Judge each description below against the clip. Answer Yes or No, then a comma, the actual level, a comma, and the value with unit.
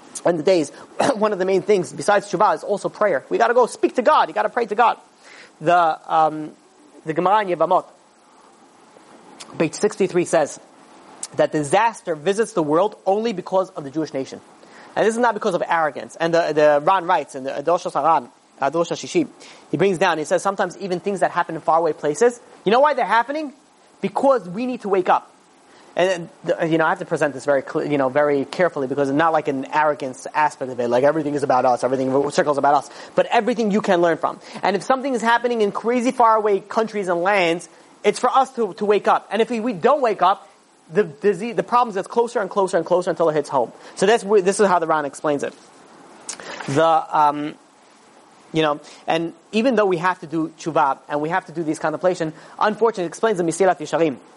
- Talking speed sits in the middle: No, fast, 210 wpm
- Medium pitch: Yes, medium, 180 Hz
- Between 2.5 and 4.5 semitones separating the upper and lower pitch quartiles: No, wide, 5.4 semitones